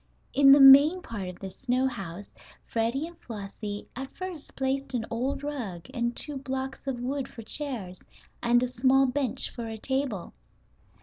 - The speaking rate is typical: Yes, average, 170 wpm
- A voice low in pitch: No, very high, 255 Hz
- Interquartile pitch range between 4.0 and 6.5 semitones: No, average, 3.4 semitones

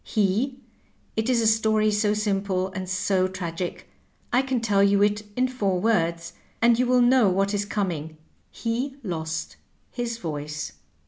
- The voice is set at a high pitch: Yes, high, 205 Hz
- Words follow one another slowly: No, average, 170 wpm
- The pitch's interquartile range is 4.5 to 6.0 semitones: No, average, 3.9 semitones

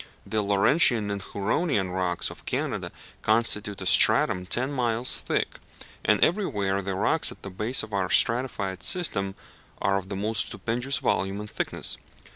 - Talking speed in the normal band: Yes, average, 155 wpm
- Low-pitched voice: Yes, low, 105 Hz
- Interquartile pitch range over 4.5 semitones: No, average, 3.6 semitones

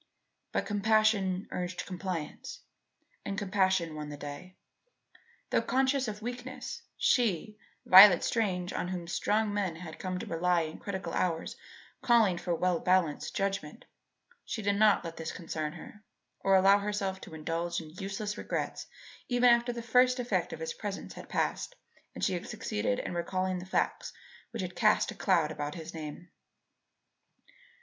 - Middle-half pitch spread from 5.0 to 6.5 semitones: No, average, 3.8 semitones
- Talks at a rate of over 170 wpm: No, average, 155 wpm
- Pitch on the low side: No, medium, 185 Hz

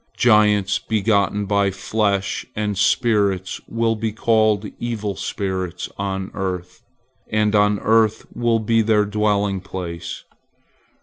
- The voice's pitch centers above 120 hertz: No, low, 105 Hz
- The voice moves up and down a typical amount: No, narrow, 2.1 semitones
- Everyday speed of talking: No, slow, 120 wpm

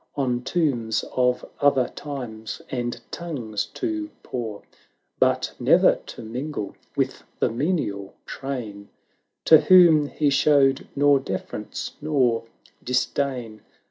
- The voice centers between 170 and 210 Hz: No, low, 130 Hz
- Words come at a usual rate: No, slow, 110 wpm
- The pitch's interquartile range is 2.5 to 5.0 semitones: Yes, average, 4.2 semitones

